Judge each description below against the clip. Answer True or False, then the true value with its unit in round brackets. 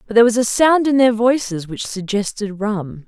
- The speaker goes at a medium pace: False (215 wpm)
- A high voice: True (220 Hz)